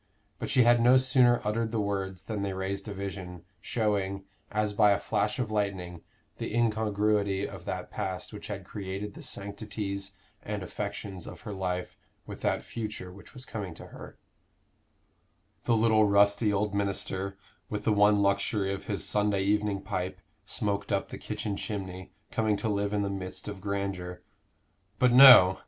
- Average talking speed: Yes, average, 170 wpm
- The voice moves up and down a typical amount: No, narrow, 1.7 semitones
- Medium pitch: No, low, 100 Hz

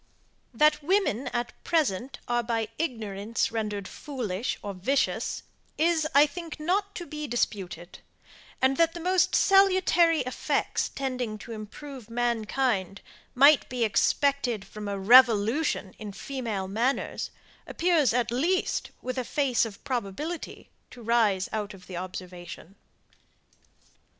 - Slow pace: Yes, slow, 125 wpm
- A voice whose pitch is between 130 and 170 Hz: No, high, 245 Hz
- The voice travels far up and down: Yes, wide, 6.1 semitones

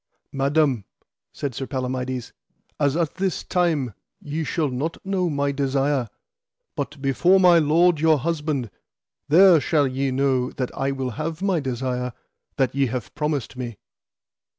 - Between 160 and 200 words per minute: No, average, 145 wpm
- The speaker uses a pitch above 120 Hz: Yes, medium, 140 Hz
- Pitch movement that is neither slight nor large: Yes, average, 3.6 semitones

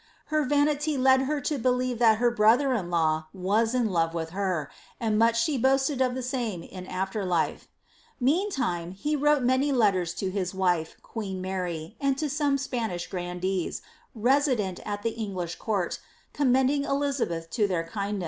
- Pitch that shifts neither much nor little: No, wide, 6.3 semitones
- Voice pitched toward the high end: Yes, high, 225 Hz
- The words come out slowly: No, average, 165 wpm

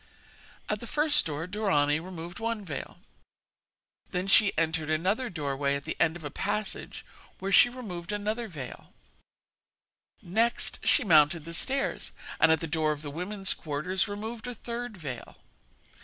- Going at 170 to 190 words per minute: No, average, 155 wpm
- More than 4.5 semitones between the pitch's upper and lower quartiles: Yes, wide, 5.5 semitones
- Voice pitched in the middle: Yes, medium, 180 Hz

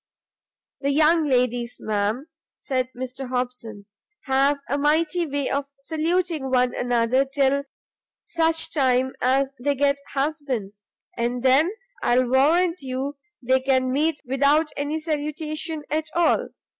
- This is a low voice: No, very high, 275 Hz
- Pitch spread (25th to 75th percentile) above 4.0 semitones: No, average, 3.1 semitones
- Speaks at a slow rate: Yes, slow, 125 wpm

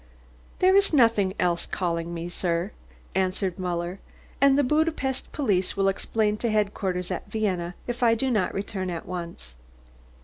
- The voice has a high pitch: Yes, high, 195 Hz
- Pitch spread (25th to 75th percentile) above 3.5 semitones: Yes, average, 4.7 semitones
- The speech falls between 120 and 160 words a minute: Yes, average, 150 wpm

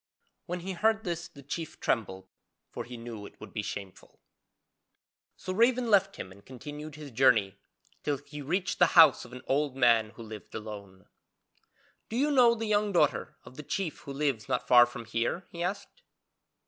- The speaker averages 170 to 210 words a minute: Yes, average, 185 wpm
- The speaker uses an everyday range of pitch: No, wide, 7.7 semitones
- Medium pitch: Yes, medium, 145 Hz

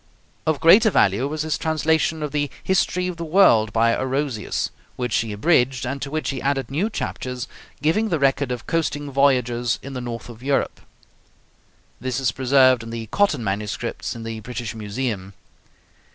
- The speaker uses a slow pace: No, average, 170 wpm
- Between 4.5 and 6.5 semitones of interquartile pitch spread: Yes, average, 4.8 semitones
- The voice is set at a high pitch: No, low, 130 Hz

